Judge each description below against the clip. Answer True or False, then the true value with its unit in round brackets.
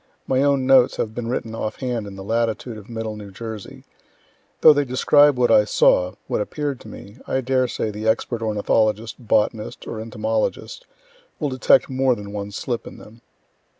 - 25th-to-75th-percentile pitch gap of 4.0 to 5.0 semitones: False (3.2 semitones)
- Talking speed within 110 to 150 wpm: False (185 wpm)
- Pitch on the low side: True (115 Hz)